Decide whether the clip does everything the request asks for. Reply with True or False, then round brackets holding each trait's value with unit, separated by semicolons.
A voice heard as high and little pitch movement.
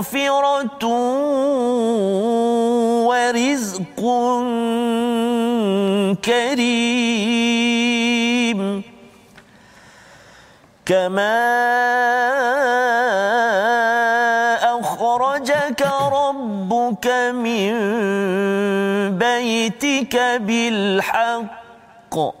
True (235 Hz; 1.5 semitones)